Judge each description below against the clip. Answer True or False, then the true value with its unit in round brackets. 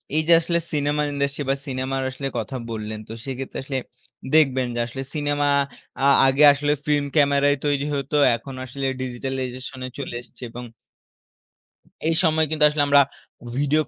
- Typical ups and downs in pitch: False (2.0 semitones)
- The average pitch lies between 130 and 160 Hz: True (140 Hz)